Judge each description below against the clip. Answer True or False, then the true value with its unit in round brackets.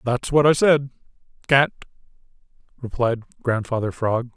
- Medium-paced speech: False (95 wpm)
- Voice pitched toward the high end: False (125 Hz)